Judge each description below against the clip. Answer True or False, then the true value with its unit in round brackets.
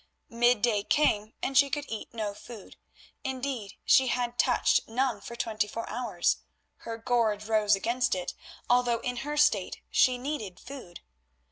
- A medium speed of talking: True (150 wpm)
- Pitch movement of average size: True (3.2 semitones)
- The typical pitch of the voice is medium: False (235 Hz)